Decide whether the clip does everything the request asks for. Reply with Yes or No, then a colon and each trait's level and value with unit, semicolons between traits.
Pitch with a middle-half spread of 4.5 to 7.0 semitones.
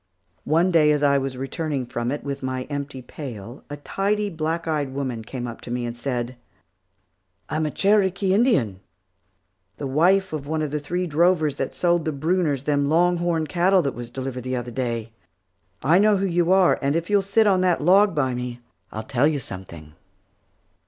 Yes: wide, 5.4 semitones